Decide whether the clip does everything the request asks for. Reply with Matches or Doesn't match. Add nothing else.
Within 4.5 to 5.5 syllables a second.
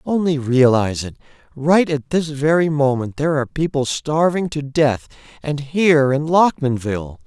Matches